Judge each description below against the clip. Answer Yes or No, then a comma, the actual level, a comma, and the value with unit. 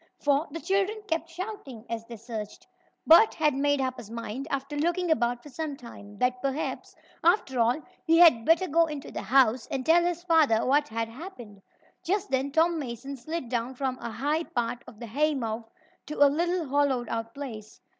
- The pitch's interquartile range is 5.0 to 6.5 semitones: Yes, wide, 5.4 semitones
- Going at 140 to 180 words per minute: No, average, 190 wpm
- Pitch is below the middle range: No, very high, 275 Hz